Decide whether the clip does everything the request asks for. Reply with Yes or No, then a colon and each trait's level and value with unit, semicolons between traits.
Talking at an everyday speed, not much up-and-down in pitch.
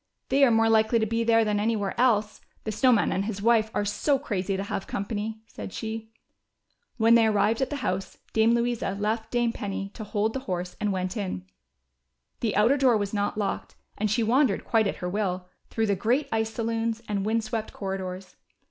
No: fast, 210 wpm; narrow, 2.3 semitones